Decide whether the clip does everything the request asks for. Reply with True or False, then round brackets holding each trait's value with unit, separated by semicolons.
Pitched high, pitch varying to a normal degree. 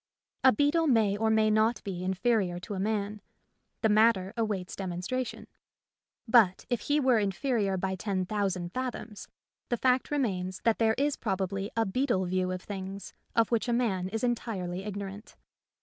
True (210 Hz; 3.7 semitones)